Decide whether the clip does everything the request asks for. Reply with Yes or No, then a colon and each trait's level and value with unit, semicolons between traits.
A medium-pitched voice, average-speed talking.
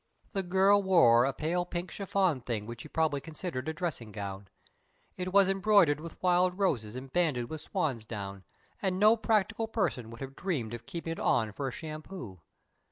Yes: medium, 160 Hz; average, 180 wpm